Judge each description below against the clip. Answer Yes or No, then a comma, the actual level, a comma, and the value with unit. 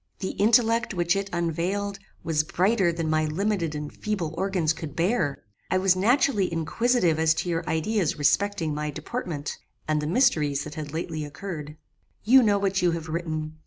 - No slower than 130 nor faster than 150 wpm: No, average, 170 wpm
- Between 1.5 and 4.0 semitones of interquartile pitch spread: No, average, 4.4 semitones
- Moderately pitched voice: Yes, medium, 170 Hz